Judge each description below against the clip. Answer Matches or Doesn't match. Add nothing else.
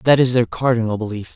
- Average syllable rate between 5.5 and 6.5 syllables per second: Matches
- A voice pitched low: Matches